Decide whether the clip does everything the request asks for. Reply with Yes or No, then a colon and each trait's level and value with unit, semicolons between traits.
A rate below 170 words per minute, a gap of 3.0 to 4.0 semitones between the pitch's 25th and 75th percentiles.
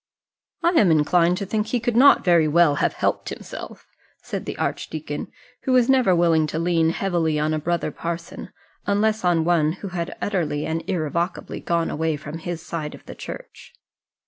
No: average, 180 wpm; average, 3.3 semitones